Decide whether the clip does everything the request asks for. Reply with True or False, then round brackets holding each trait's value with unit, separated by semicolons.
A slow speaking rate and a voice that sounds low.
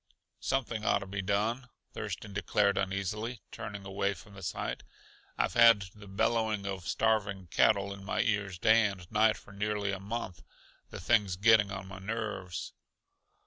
False (160 wpm; 100 Hz)